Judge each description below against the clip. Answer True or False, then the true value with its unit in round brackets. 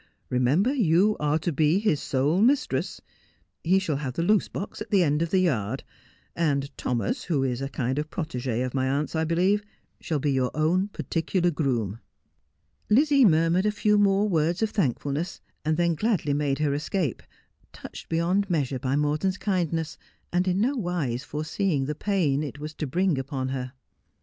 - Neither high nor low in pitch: True (160 Hz)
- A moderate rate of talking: True (180 wpm)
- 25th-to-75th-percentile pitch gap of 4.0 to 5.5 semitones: True (5.2 semitones)